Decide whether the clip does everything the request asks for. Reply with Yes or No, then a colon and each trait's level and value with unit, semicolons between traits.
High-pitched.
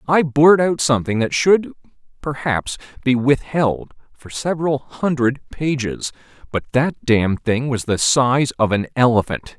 No: low, 130 Hz